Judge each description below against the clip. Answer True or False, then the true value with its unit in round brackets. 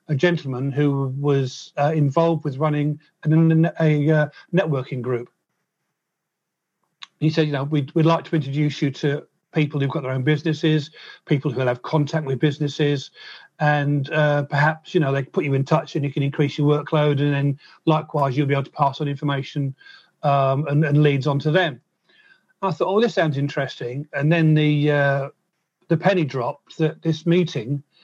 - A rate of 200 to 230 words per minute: False (185 wpm)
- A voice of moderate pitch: True (150 Hz)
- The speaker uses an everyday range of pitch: False (2.1 semitones)